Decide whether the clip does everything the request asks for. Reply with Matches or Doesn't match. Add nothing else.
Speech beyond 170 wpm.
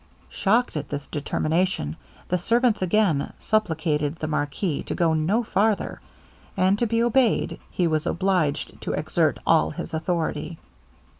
Doesn't match